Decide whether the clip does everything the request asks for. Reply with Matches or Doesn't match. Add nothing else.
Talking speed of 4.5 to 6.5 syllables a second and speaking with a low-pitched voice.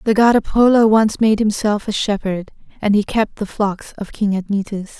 Doesn't match